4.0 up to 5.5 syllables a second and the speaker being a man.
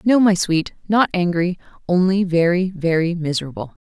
No: 5.0 syllables/s; female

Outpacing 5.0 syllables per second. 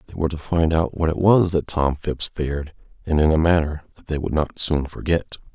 Yes: 5.7 syllables/s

